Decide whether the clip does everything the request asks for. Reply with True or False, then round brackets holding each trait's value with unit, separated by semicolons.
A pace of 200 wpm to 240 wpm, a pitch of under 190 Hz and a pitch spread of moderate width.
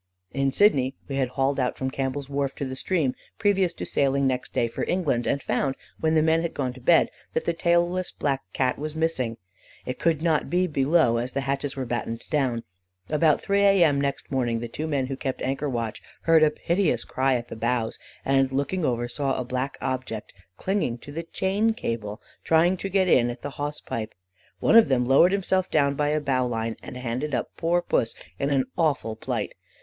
True (205 wpm; 140 Hz; 4.3 semitones)